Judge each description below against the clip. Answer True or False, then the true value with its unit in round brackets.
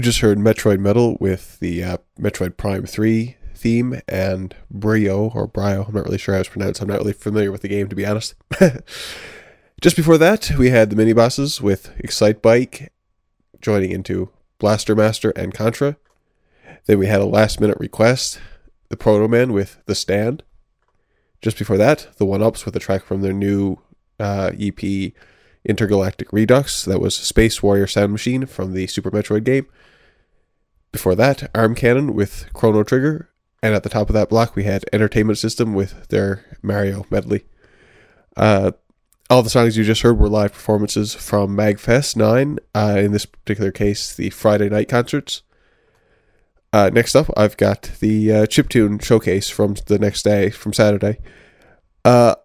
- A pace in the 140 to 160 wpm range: False (170 wpm)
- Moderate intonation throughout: False (2.3 semitones)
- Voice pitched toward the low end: True (105 Hz)